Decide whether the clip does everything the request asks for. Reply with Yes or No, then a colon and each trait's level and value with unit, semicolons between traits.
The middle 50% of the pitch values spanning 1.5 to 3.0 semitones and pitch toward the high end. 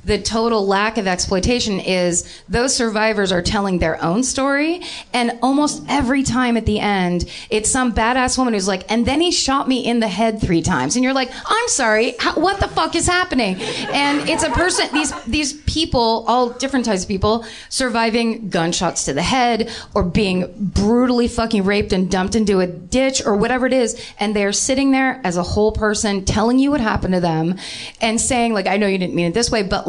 No: average, 4.5 semitones; high, 230 Hz